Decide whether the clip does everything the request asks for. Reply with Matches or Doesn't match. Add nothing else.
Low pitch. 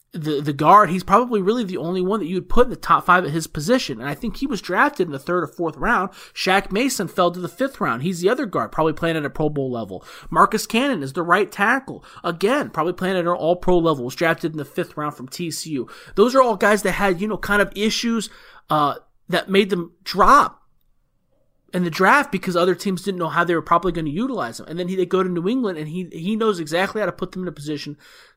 Doesn't match